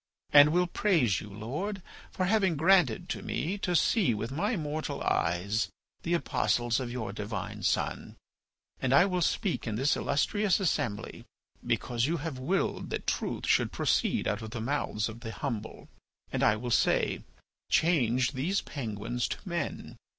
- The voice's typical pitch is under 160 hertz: Yes, low, 135 Hz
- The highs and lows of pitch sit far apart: Yes, wide, 7.7 semitones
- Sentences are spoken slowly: No, average, 160 wpm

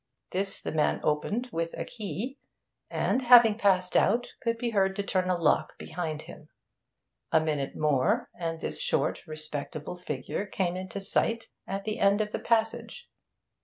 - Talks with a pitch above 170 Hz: Yes, high, 190 Hz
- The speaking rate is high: No, average, 165 wpm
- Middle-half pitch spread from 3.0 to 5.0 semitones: No, wide, 5.5 semitones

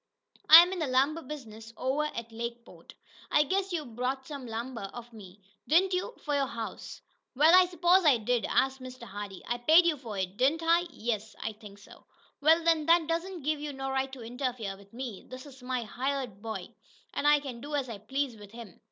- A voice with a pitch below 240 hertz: No, very high, 260 Hz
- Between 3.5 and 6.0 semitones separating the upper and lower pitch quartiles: Yes, average, 4.9 semitones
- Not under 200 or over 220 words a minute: Yes, fast, 205 wpm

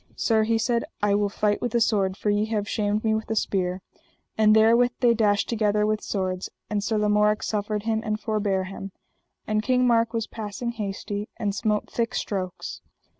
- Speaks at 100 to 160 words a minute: No, average, 190 wpm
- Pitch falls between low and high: No, high, 215 Hz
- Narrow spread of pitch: Yes, narrow, 1.6 semitones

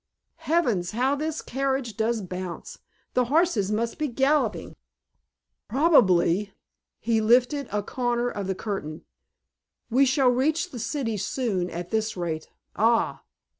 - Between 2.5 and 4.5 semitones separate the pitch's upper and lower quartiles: No, average, 5.1 semitones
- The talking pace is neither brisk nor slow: No, slow, 130 wpm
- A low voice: No, high, 235 Hz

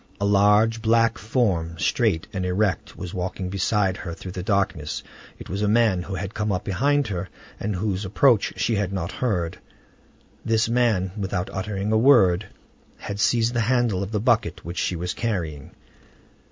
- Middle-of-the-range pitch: No, low, 100 Hz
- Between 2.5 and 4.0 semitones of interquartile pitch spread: Yes, average, 3.4 semitones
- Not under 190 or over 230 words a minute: No, average, 175 wpm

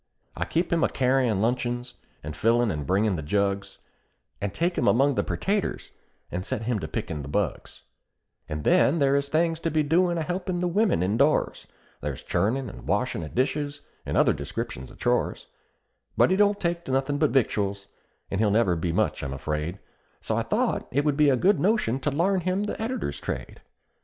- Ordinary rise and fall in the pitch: No, wide, 8.8 semitones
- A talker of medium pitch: No, low, 130 Hz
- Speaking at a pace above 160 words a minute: Yes, average, 195 wpm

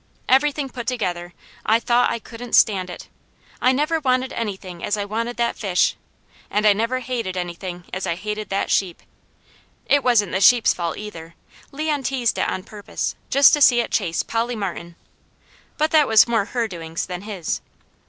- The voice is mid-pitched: No, high, 220 Hz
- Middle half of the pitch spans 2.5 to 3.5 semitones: No, average, 5.1 semitones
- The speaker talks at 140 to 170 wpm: No, average, 180 wpm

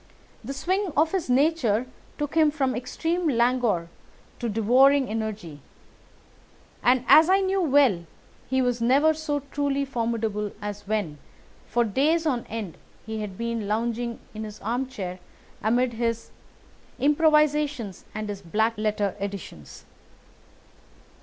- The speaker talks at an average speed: No, slow, 125 wpm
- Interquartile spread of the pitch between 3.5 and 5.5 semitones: Yes, average, 5.1 semitones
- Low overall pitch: No, high, 240 Hz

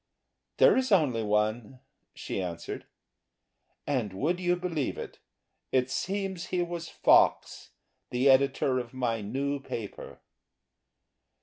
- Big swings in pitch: Yes, wide, 7.1 semitones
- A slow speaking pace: Yes, slow, 115 wpm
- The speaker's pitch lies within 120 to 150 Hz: Yes, low, 135 Hz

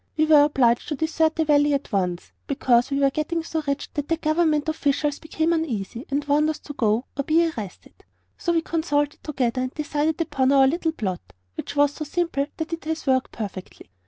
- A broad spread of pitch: No, average, 3.1 semitones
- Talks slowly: No, fast, 205 wpm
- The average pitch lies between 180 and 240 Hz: No, very high, 290 Hz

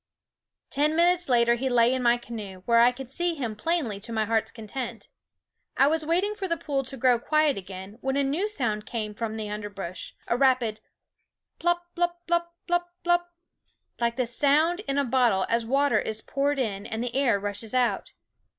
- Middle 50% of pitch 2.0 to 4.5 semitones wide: No, wide, 5.6 semitones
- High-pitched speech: Yes, very high, 250 Hz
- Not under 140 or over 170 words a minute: No, average, 190 wpm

